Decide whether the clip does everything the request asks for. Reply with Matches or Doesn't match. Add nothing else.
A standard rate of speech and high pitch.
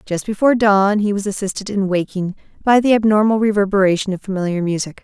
Matches